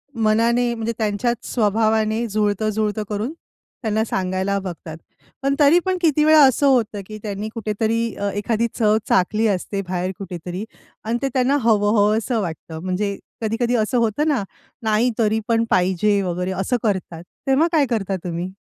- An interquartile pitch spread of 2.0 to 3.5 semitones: Yes, average, 2.9 semitones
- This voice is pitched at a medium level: No, high, 215 Hz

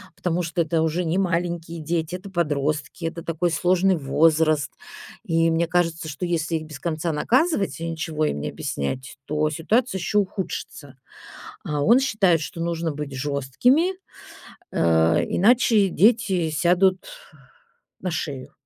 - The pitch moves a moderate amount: Yes, average, 3.0 semitones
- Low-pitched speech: No, medium, 165 Hz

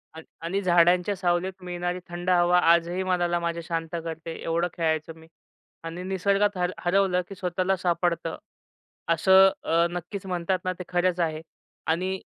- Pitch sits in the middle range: Yes, medium, 175 Hz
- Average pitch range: No, narrow, 1.6 semitones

